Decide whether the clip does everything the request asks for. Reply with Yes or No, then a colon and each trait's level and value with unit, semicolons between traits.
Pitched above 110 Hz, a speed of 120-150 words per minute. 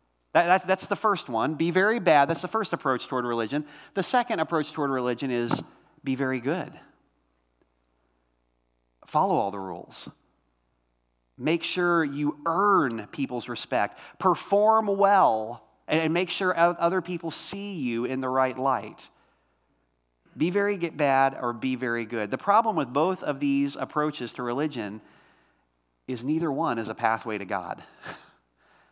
Yes: low, 135 Hz; average, 145 wpm